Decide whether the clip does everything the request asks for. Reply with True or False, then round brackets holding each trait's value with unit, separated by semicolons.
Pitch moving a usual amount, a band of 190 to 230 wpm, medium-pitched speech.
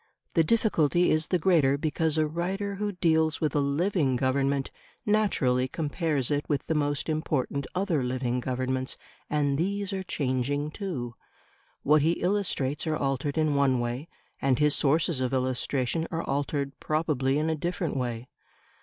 False (3.7 semitones; 155 wpm; 150 Hz)